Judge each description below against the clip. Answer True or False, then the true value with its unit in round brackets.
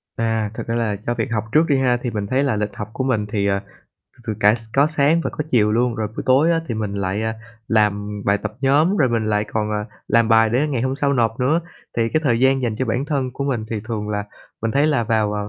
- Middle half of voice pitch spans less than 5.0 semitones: True (3.9 semitones)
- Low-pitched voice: True (115 Hz)